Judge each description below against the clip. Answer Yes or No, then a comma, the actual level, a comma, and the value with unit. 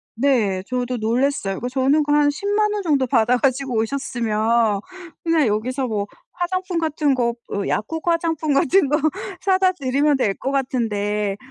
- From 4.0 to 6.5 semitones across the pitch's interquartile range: Yes, average, 5.3 semitones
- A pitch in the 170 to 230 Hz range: No, very high, 265 Hz